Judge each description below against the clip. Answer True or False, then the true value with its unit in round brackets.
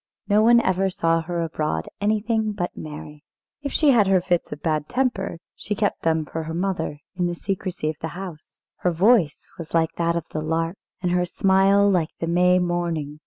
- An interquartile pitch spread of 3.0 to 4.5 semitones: True (3.3 semitones)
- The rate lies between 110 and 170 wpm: False (200 wpm)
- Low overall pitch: False (175 Hz)